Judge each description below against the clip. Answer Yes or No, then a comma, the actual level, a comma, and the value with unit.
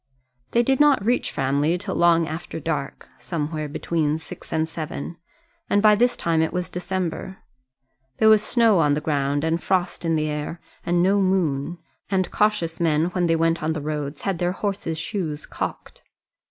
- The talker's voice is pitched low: No, medium, 165 Hz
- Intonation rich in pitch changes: No, average, 3.6 semitones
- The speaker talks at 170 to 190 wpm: Yes, average, 180 wpm